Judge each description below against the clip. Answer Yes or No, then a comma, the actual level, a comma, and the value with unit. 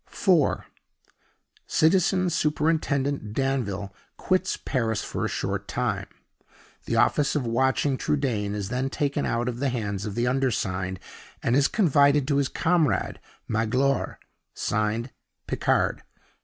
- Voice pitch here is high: No, low, 130 Hz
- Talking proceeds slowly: Yes, slow, 125 wpm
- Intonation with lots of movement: No, average, 4.7 semitones